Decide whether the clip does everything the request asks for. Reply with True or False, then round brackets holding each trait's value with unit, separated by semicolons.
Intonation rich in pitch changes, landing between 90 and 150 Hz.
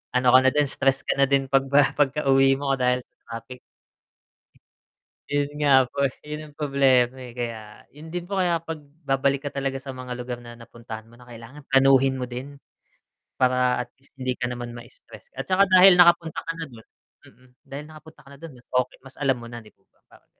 False (2.6 semitones; 135 Hz)